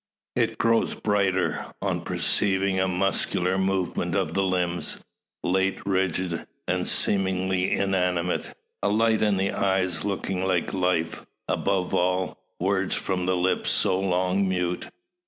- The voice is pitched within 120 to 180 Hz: No, very low, 95 Hz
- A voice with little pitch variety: Yes, narrow, 1.2 semitones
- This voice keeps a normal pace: No, slow, 130 wpm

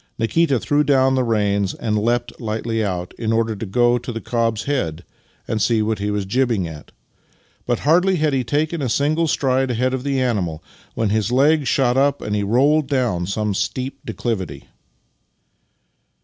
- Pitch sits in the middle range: No, low, 120 Hz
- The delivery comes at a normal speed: Yes, average, 175 wpm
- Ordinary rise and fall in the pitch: Yes, average, 4.0 semitones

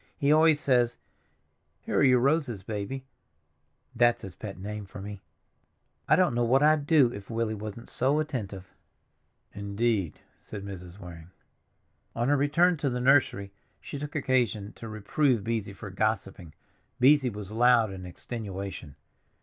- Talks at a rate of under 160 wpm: Yes, average, 145 wpm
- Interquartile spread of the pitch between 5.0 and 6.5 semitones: Yes, average, 5.3 semitones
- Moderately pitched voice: No, low, 115 Hz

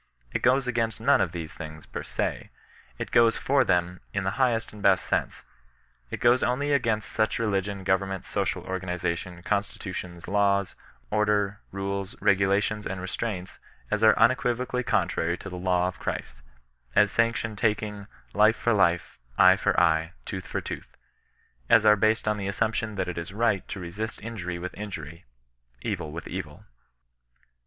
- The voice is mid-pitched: No, low, 100 Hz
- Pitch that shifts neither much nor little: Yes, average, 3.4 semitones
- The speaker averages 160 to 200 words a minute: Yes, average, 175 wpm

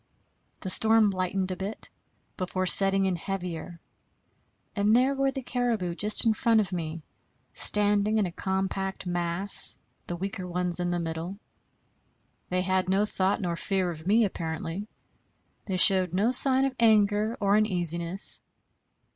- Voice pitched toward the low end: No, high, 190 Hz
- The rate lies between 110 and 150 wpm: Yes, average, 145 wpm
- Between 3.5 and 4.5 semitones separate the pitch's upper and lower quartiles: No, average, 3.0 semitones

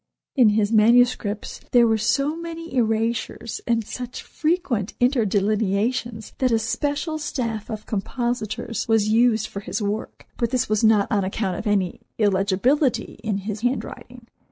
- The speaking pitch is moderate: No, high, 225 Hz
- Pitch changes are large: No, average, 2.8 semitones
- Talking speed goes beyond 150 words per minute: No, average, 145 wpm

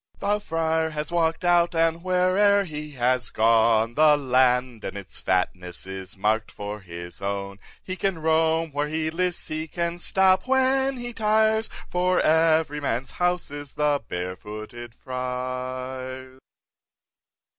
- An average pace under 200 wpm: Yes, average, 140 wpm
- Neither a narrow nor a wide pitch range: No, wide, 6.6 semitones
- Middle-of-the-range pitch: Yes, medium, 150 Hz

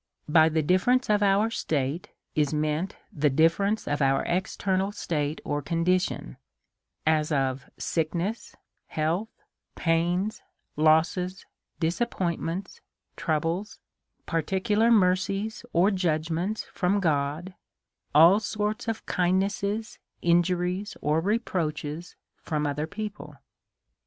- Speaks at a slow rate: Yes, slow, 105 wpm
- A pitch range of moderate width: Yes, average, 4.3 semitones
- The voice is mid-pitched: Yes, medium, 175 Hz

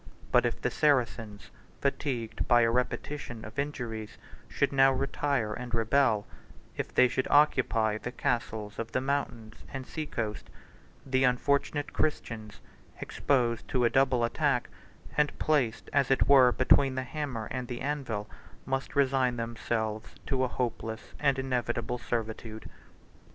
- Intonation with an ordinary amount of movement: Yes, average, 3.2 semitones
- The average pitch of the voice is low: Yes, low, 125 Hz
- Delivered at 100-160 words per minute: Yes, average, 140 wpm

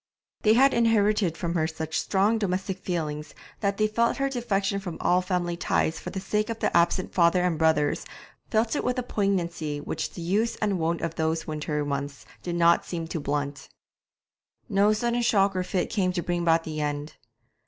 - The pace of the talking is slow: No, average, 195 wpm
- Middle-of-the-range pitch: Yes, medium, 180 Hz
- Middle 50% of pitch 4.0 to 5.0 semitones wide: Yes, average, 4.4 semitones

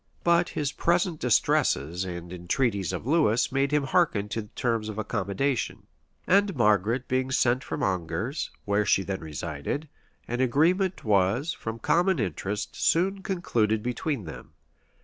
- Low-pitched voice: Yes, low, 120 Hz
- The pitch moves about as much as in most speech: No, wide, 7.0 semitones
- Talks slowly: No, average, 150 wpm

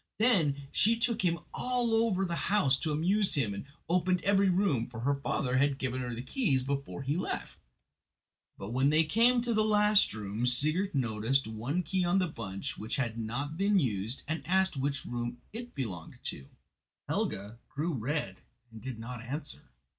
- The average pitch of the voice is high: No, medium, 145 Hz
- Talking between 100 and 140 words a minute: No, average, 180 wpm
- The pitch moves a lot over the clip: Yes, wide, 7.7 semitones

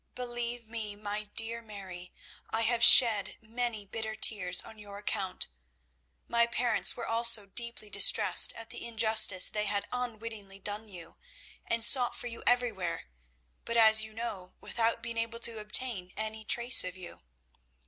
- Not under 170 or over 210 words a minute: No, average, 155 wpm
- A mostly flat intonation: Yes, narrow, 2.3 semitones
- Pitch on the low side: No, high, 220 Hz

